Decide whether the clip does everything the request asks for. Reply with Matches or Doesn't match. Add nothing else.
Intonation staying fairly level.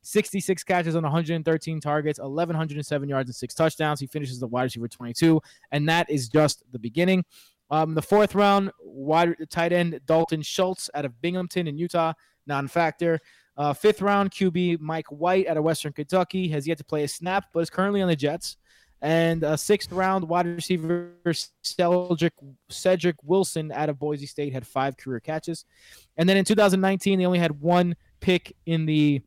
Doesn't match